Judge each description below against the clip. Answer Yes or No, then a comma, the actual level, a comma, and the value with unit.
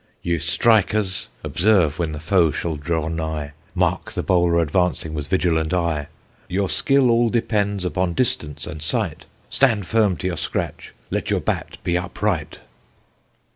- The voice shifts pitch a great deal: No, average, 4.1 semitones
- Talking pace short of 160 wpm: Yes, average, 150 wpm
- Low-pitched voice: Yes, very low, 85 Hz